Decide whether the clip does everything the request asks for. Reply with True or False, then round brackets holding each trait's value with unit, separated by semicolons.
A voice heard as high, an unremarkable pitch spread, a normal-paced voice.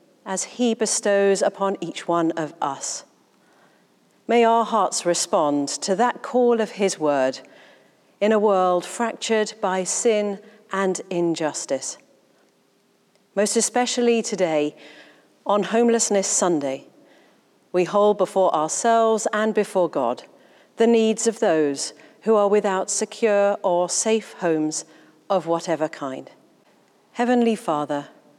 False (200 Hz; 4.6 semitones; 115 wpm)